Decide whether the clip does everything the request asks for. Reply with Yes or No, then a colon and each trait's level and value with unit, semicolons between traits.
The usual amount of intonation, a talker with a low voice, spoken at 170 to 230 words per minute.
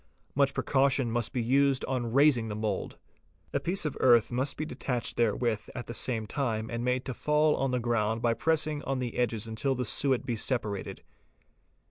Yes: average, 3.0 semitones; low, 125 Hz; average, 190 wpm